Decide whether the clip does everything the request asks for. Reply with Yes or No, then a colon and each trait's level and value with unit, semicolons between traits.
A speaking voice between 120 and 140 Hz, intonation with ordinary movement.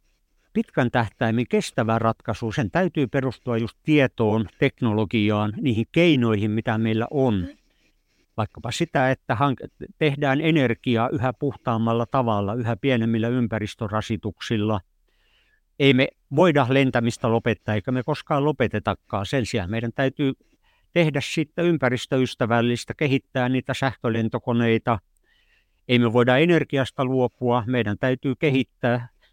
Yes: low, 125 Hz; average, 3.4 semitones